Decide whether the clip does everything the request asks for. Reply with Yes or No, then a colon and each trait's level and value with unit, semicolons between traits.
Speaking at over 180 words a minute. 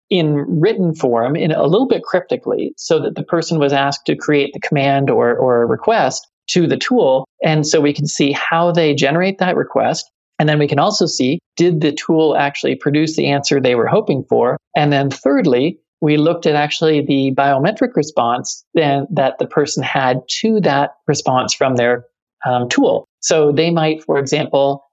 Yes: average, 190 wpm